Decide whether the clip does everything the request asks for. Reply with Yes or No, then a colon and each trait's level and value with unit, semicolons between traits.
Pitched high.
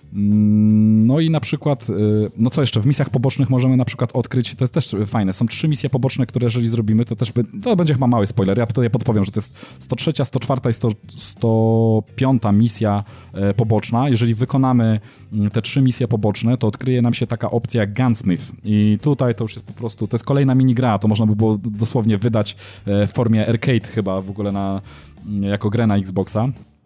No: low, 115 Hz